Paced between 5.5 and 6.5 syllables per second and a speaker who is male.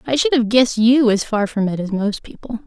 No: 5.6 syllables/s; female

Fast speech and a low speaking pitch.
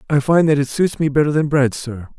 No: fast, 275 wpm; medium, 145 Hz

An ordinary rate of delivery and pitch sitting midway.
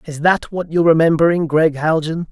Yes: average, 180 wpm; medium, 160 Hz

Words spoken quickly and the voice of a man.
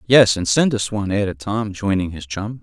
Yes: fast, 230 wpm; male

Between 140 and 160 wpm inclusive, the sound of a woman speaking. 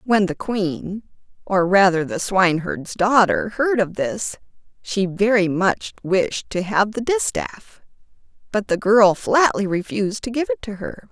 Yes: average, 145 wpm; female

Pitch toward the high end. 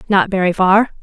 Yes: high, 195 Hz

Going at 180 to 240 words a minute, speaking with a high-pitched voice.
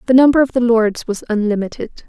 Yes: average, 200 wpm; high, 230 Hz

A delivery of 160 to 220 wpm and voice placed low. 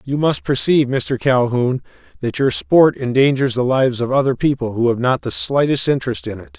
Yes: average, 200 wpm; low, 130 Hz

